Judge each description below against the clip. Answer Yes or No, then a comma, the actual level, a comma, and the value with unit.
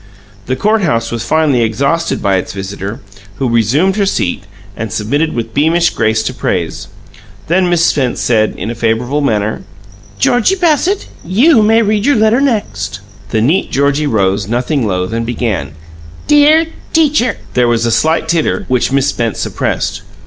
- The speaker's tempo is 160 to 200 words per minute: Yes, average, 165 wpm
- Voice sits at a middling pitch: No, low, 130 Hz